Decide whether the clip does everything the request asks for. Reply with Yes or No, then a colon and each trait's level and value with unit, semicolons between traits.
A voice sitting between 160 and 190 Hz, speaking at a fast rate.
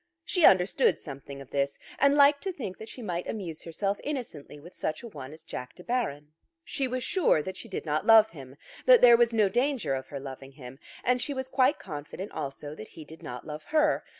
Yes: medium, 185 Hz; fast, 225 wpm